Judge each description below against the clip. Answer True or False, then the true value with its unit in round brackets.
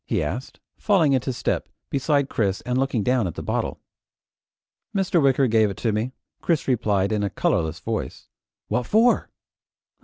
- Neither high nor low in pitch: False (125 Hz)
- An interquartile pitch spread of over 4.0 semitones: True (4.9 semitones)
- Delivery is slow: False (160 wpm)